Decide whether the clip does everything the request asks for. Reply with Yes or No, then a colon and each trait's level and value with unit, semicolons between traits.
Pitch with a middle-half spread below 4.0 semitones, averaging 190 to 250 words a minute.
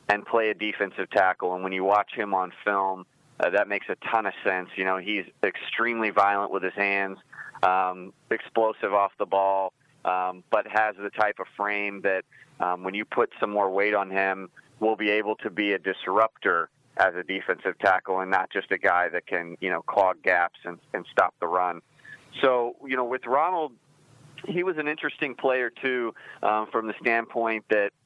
Yes: average, 3.4 semitones; average, 195 wpm